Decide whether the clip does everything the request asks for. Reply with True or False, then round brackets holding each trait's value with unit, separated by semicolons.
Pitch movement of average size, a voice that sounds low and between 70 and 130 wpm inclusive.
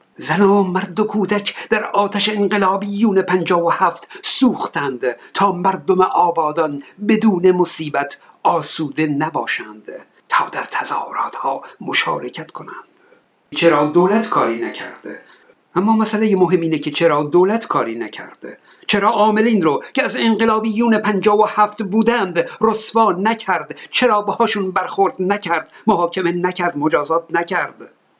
False (4.0 semitones; 195 Hz; 125 wpm)